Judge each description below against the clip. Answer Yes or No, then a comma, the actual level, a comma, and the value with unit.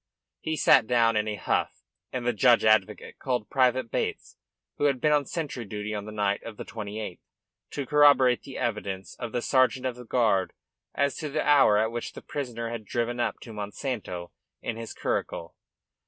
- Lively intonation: No, average, 3.4 semitones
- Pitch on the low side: Yes, low, 120 Hz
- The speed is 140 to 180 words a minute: No, average, 190 wpm